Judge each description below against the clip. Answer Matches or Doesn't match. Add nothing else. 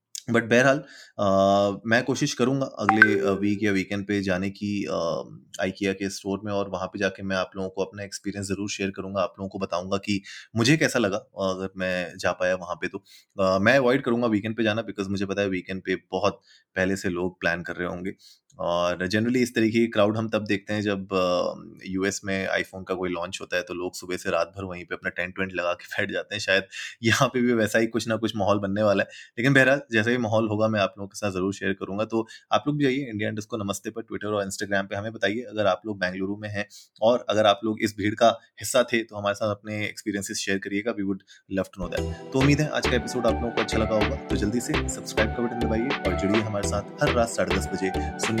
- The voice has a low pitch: Matches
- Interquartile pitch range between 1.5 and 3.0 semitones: Matches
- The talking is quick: Matches